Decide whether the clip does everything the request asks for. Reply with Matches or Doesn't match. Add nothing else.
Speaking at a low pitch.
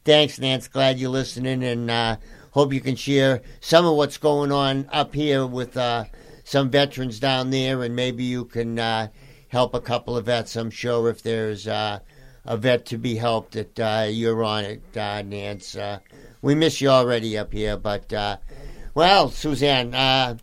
Matches